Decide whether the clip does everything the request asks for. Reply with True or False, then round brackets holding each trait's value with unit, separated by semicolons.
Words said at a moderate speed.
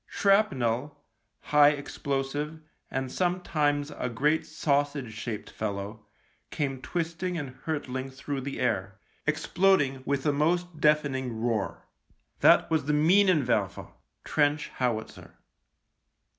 False (110 wpm)